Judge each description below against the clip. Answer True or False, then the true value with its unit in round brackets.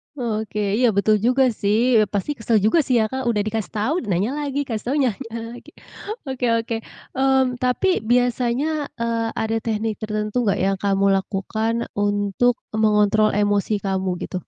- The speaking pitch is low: False (220 Hz)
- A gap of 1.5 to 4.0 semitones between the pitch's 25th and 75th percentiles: True (3.2 semitones)